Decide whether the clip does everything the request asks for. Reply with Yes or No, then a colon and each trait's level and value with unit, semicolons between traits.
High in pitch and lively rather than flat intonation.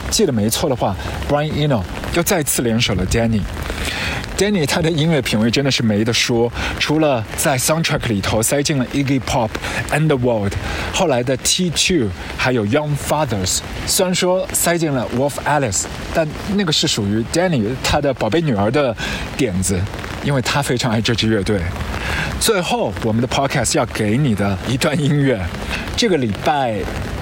No: low, 120 Hz; wide, 6.4 semitones